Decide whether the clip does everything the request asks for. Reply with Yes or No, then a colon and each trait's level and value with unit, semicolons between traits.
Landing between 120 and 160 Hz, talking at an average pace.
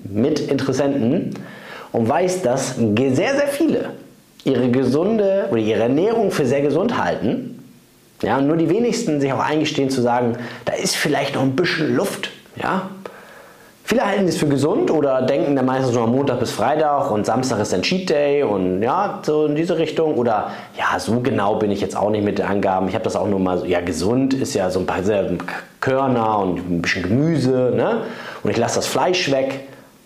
No: low, 135 Hz; fast, 195 wpm